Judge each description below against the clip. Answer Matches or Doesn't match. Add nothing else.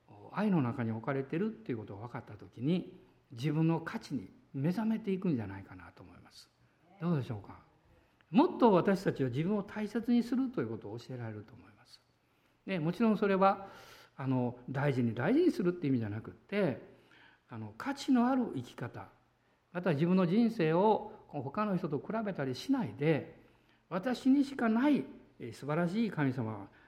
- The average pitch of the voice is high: Doesn't match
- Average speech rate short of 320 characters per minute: Doesn't match